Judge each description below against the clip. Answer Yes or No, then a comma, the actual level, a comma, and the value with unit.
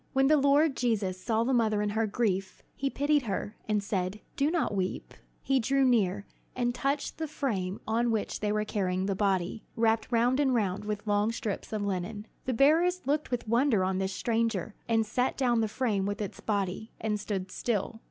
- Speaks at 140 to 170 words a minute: No, average, 200 wpm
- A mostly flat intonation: No, average, 4.0 semitones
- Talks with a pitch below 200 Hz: No, high, 220 Hz